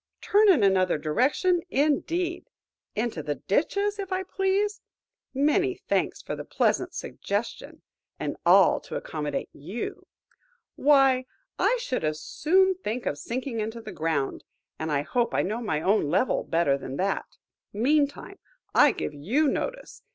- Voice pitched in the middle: No, high, 245 Hz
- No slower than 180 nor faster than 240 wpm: No, slow, 135 wpm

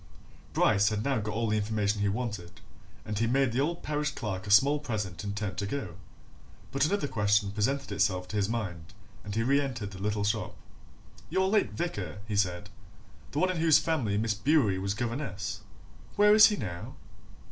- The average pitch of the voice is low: Yes, low, 110 Hz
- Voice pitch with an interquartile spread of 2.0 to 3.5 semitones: No, wide, 5.5 semitones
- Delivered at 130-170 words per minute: No, average, 190 wpm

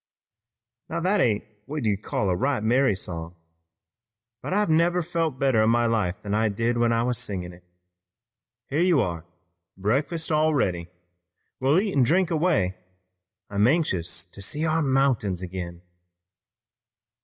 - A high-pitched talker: No, low, 120 Hz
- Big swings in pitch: Yes, wide, 8.3 semitones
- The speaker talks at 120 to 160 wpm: Yes, average, 155 wpm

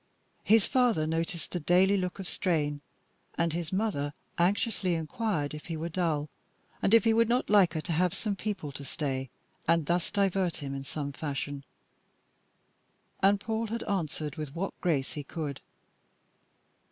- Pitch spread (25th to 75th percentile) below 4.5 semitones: No, average, 4.8 semitones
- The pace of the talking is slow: No, average, 165 wpm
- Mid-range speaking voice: Yes, medium, 170 Hz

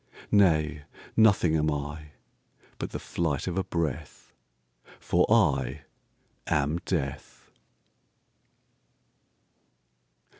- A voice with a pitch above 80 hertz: No, very low, 75 Hz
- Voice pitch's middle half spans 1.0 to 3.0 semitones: No, average, 3.4 semitones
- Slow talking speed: Yes, slow, 70 wpm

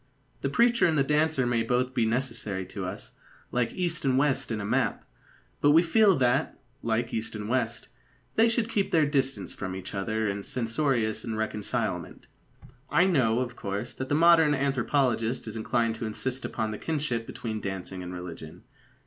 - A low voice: Yes, low, 120 Hz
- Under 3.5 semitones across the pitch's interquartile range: No, average, 4.9 semitones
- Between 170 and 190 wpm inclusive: Yes, average, 175 wpm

